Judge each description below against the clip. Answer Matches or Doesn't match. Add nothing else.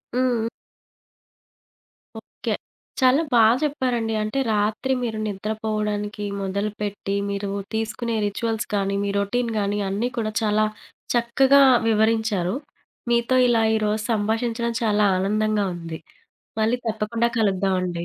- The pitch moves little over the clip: Matches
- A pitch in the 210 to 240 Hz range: Matches